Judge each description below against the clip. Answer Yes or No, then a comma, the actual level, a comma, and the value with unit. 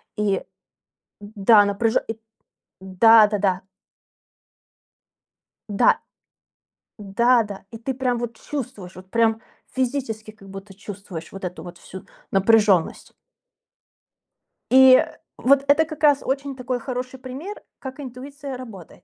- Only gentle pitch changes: No, average, 4.6 semitones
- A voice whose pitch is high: Yes, high, 225 Hz